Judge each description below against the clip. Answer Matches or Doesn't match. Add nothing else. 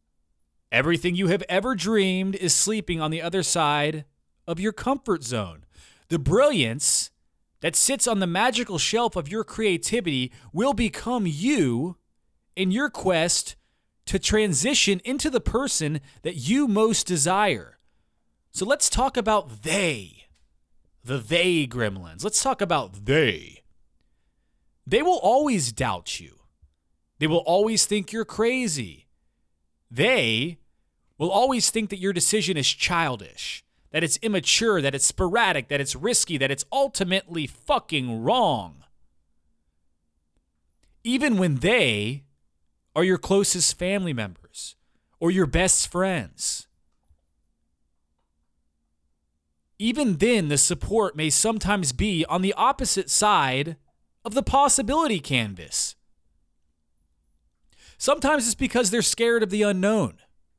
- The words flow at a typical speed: Doesn't match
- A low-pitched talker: Doesn't match